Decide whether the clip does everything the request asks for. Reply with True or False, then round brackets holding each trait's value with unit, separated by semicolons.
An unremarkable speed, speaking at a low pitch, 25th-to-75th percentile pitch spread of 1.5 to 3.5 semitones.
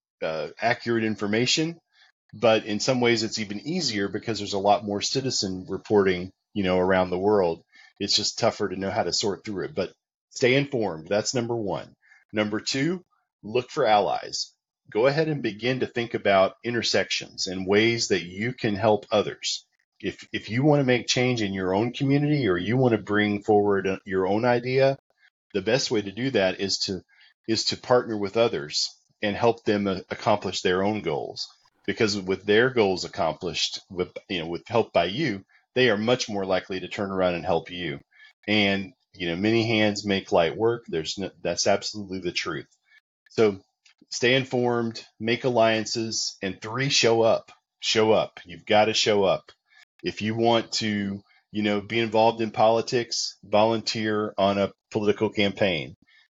True (175 wpm; 110 Hz; 2.8 semitones)